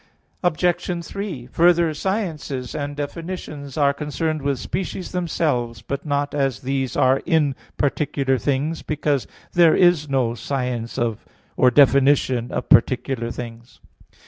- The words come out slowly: Yes, slow, 120 wpm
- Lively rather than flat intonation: No, average, 4.0 semitones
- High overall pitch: No, medium, 140 Hz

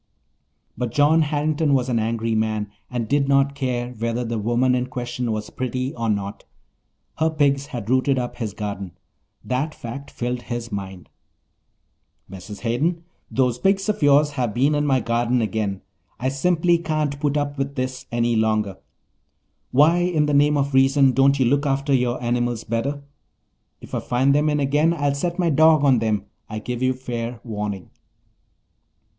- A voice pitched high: No, low, 130 Hz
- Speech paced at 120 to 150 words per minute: No, average, 170 wpm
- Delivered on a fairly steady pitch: No, average, 3.6 semitones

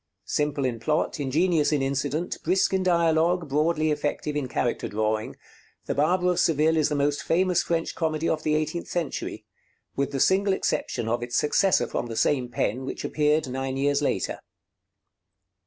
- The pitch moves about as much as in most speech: Yes, average, 3.5 semitones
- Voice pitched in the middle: Yes, medium, 150 Hz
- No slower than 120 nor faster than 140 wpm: No, average, 170 wpm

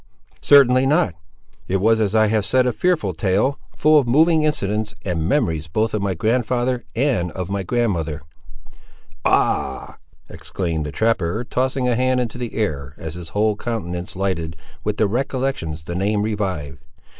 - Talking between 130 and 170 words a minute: Yes, average, 165 wpm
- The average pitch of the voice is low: Yes, low, 105 Hz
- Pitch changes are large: Yes, wide, 6.2 semitones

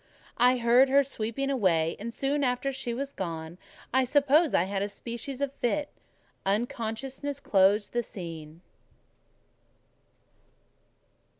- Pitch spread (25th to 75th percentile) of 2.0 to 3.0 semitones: No, wide, 5.5 semitones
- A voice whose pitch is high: Yes, high, 240 Hz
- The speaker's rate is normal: No, slow, 120 wpm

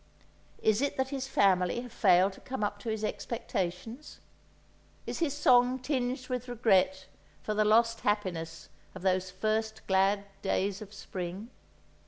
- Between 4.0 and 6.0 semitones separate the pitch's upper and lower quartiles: Yes, average, 4.5 semitones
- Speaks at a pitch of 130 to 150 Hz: No, high, 215 Hz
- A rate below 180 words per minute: Yes, average, 150 wpm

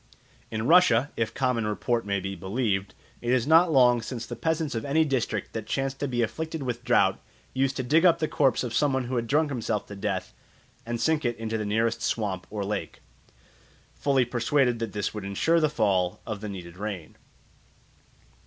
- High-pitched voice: No, low, 120 Hz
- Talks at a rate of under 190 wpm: No, average, 200 wpm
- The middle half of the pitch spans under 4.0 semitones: No, average, 4.5 semitones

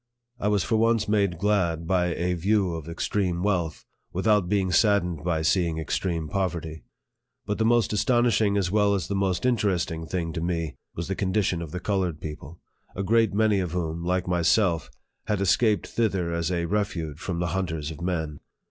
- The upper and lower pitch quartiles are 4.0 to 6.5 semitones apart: No, average, 3.6 semitones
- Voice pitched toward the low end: Yes, very low, 90 Hz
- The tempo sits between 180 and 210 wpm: Yes, average, 185 wpm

